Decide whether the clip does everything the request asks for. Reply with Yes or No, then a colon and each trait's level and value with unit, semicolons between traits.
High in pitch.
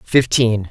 No: low, 115 Hz